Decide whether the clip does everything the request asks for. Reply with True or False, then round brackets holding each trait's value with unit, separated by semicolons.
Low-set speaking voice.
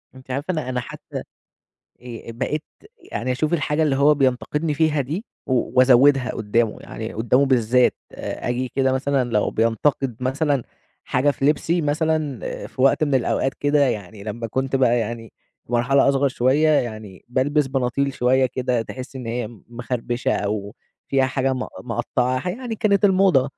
True (130 Hz)